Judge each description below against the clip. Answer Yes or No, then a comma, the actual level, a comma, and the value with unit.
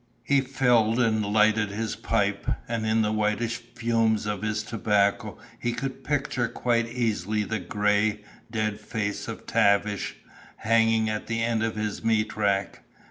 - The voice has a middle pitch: No, low, 110 Hz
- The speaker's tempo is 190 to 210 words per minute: No, average, 150 wpm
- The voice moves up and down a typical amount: No, narrow, 1.7 semitones